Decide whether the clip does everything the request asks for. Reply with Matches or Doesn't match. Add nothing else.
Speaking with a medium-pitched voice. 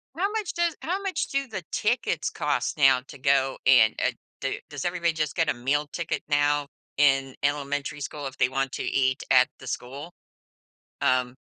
Matches